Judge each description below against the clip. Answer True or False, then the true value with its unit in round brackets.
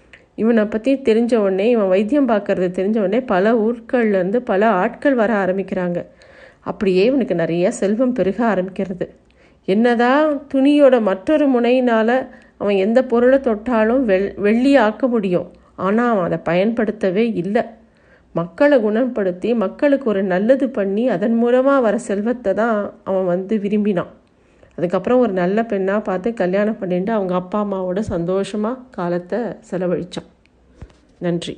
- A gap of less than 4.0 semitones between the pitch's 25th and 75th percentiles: False (4.3 semitones)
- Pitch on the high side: True (210 Hz)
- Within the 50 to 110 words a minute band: False (120 wpm)